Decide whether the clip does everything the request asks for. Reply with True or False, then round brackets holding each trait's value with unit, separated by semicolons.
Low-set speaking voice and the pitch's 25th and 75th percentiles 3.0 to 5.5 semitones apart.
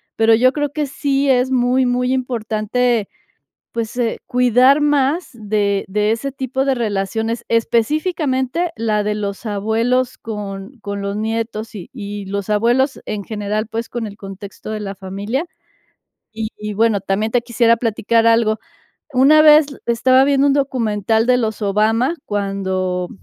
False (225 Hz; 3.6 semitones)